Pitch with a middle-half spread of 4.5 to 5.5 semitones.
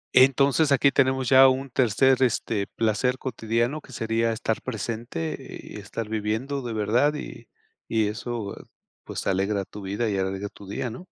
No: average, 3.8 semitones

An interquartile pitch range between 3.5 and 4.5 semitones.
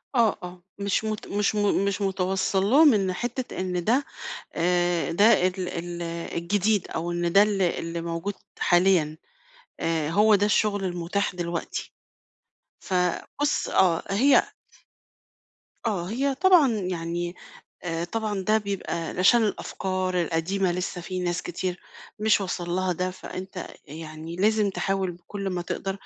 No: average, 2.9 semitones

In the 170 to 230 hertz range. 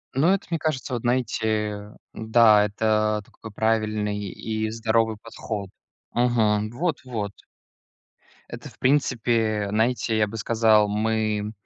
No: low, 110 Hz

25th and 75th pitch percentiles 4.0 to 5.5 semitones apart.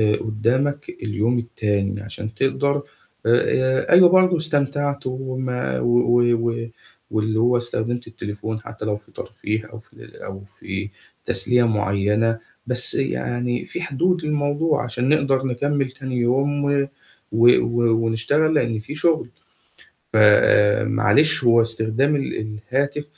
Yes: average, 4.4 semitones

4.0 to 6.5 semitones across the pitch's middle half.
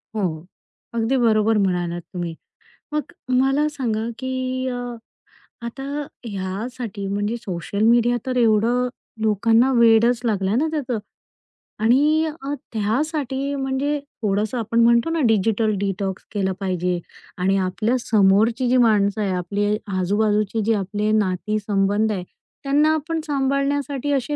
Yes: average, 4.4 semitones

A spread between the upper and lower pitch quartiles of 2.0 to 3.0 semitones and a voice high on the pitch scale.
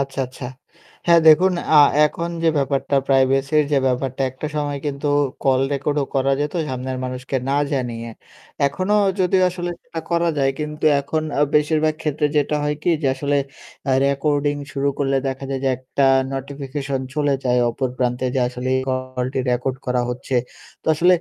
No: narrow, 2.4 semitones; medium, 140 Hz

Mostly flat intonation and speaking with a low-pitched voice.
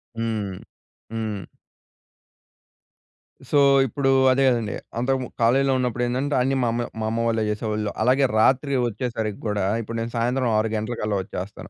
No: average, 3.1 semitones; low, 115 Hz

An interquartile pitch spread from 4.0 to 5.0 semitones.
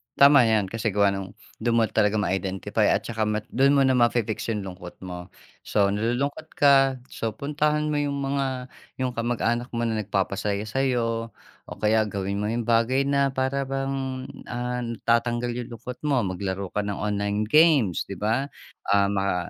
Yes: average, 4.5 semitones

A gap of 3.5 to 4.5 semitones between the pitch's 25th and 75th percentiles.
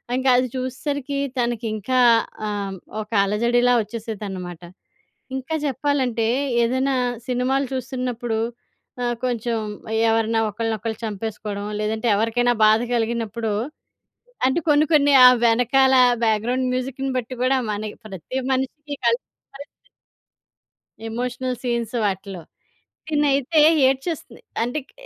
No: average, 3.0 semitones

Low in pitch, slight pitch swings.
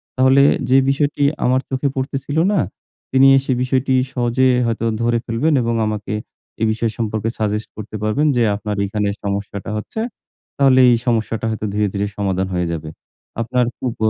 No: low, 115 Hz; average, 3.7 semitones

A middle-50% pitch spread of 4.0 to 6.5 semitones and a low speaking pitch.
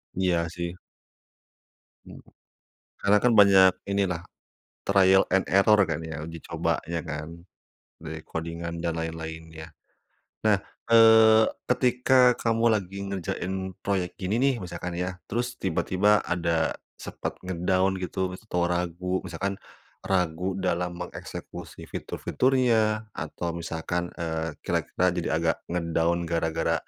No: average, 2.9 semitones; very low, 90 Hz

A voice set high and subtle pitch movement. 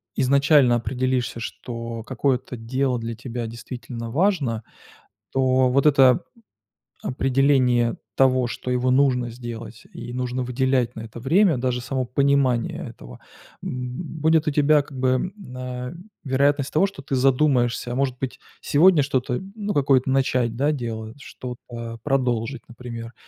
No: low, 130 Hz; narrow, 2.3 semitones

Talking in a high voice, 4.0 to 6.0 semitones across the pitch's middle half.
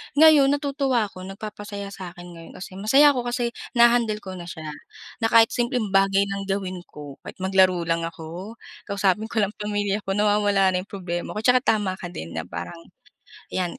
No: high, 200 Hz; average, 3.5 semitones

